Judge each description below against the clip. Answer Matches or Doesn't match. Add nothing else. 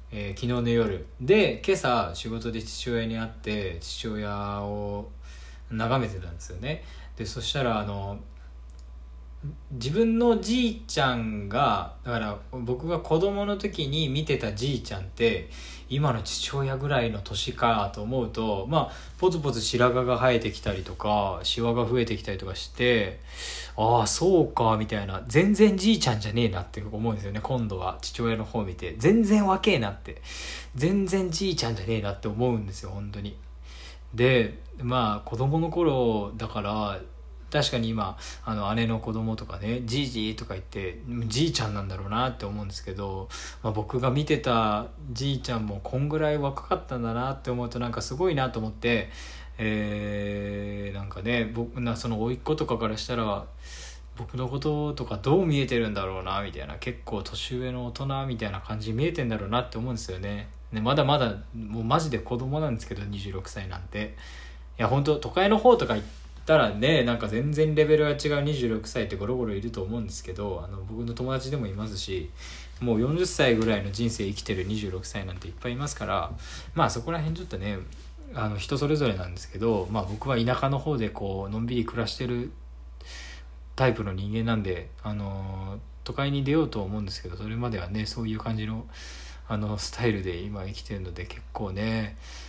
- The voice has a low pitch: Matches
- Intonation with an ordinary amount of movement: Matches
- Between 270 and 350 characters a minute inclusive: Matches